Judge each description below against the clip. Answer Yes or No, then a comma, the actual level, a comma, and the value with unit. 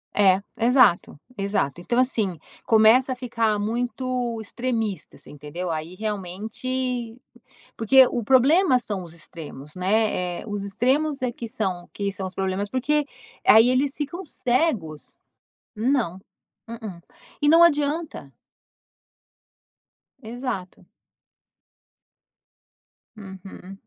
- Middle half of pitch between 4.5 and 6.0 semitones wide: Yes, average, 5.1 semitones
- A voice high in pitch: Yes, high, 225 Hz